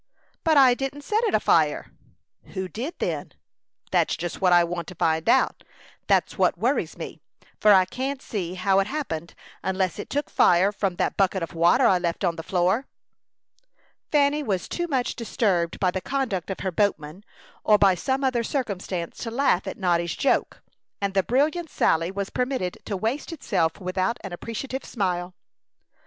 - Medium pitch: No, high, 195 Hz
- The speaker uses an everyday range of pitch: No, wide, 6.4 semitones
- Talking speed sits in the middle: Yes, average, 175 wpm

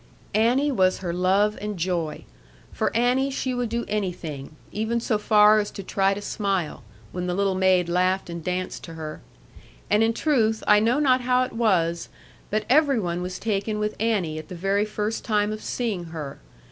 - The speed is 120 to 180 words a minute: No, average, 190 wpm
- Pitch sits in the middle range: No, high, 205 Hz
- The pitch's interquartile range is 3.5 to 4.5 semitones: Yes, average, 3.9 semitones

